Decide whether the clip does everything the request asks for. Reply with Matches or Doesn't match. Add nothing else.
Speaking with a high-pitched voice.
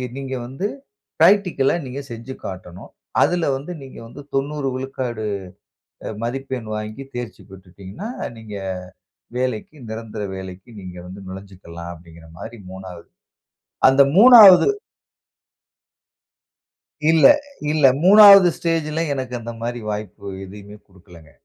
Doesn't match